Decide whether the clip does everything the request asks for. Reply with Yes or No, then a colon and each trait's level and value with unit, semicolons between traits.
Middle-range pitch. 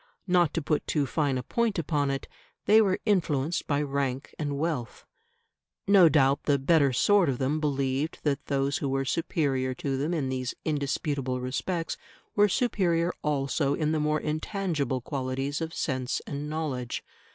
Yes: medium, 145 Hz